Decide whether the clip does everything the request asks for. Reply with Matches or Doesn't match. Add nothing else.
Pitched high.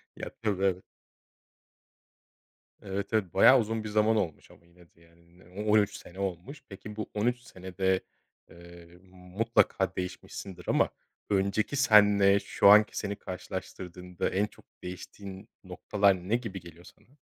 Doesn't match